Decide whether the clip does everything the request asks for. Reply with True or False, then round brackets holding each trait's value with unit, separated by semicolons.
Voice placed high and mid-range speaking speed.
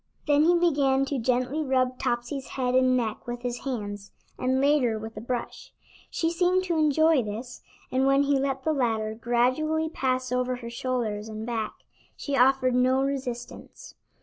True (255 Hz; 170 wpm)